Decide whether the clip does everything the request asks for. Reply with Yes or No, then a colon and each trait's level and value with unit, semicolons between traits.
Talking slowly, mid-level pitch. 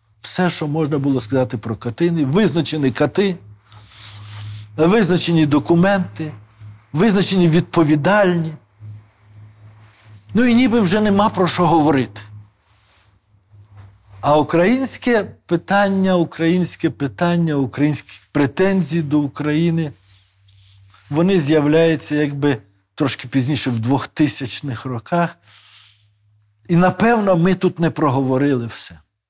Yes: slow, 95 wpm; medium, 145 Hz